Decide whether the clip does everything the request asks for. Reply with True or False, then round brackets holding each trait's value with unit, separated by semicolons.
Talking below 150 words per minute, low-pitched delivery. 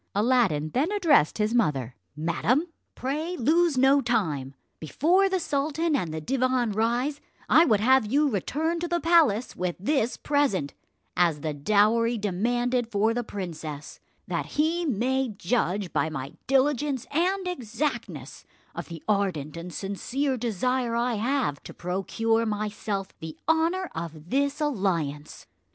False (140 wpm; 230 Hz)